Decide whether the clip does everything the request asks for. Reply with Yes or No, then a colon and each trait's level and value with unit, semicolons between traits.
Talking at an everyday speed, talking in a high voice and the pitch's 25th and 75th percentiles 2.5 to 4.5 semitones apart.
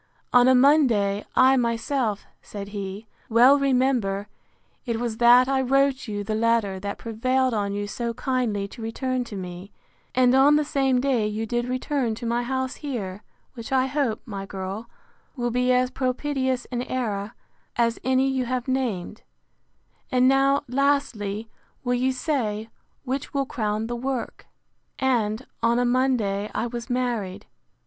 Yes: average, 155 wpm; high, 245 Hz; average, 3.4 semitones